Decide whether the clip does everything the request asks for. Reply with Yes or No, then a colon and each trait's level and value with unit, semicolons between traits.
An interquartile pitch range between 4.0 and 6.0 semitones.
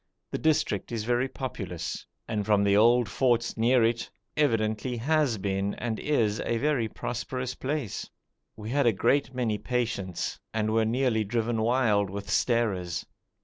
No: average, 3.0 semitones